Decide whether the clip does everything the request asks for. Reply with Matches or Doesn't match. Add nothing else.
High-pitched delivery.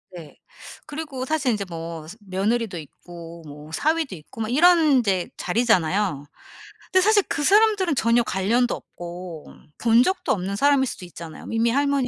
Matches